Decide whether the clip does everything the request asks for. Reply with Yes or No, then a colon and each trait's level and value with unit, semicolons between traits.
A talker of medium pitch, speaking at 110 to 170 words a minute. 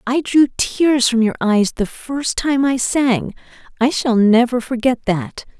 No: high, 245 Hz; average, 160 wpm